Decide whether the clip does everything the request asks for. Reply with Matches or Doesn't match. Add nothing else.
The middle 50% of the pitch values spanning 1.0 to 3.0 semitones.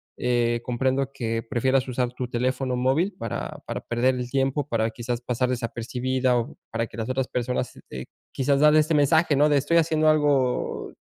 Matches